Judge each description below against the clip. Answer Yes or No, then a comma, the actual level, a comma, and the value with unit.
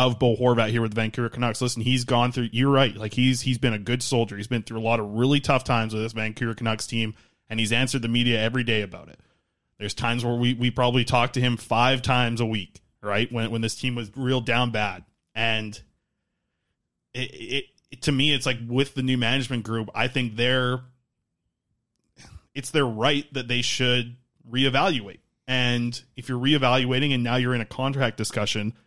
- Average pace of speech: No, fast, 210 wpm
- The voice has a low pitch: Yes, low, 120 Hz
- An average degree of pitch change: No, narrow, 2.1 semitones